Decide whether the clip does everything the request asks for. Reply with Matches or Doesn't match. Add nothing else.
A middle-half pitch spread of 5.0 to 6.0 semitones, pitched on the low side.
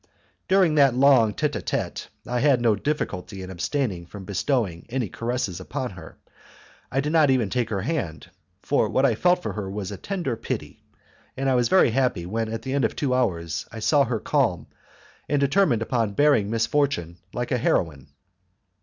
Matches